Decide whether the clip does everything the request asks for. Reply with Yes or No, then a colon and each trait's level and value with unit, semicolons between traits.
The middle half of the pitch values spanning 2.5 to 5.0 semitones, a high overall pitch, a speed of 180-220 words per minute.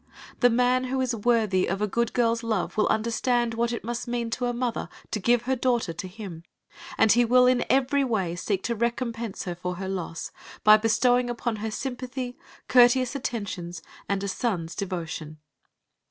Yes: average, 3.8 semitones; high, 230 Hz; average, 185 wpm